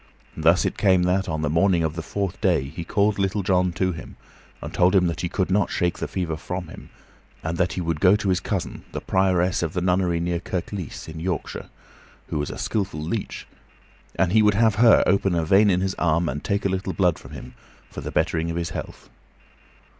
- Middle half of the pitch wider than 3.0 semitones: No, narrow, 2.4 semitones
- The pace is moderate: No, fast, 225 wpm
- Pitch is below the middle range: Yes, very low, 90 Hz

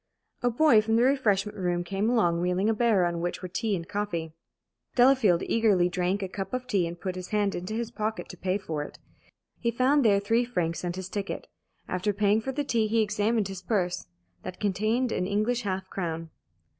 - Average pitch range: Yes, average, 3.9 semitones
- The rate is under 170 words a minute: No, fast, 205 wpm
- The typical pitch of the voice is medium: No, high, 200 Hz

